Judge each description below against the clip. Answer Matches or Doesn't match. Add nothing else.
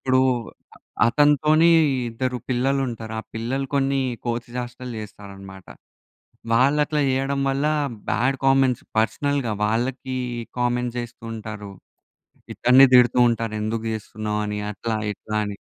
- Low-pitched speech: Matches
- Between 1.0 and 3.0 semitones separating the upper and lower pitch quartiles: Doesn't match